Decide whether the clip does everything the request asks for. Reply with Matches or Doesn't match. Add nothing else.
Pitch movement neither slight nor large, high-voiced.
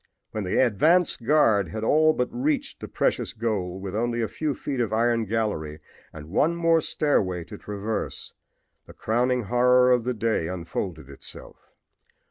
Doesn't match